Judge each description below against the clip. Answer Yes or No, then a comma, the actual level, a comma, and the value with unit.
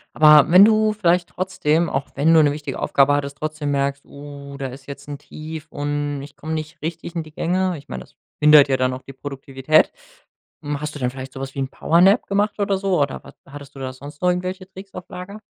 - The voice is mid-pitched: Yes, medium, 150 Hz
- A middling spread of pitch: Yes, average, 4.1 semitones